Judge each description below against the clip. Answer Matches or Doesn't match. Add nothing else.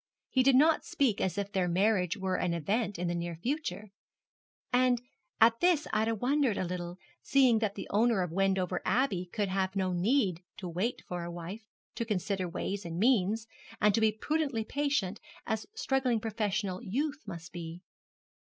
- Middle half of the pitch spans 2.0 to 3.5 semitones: Doesn't match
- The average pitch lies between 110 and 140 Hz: Doesn't match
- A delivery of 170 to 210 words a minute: Matches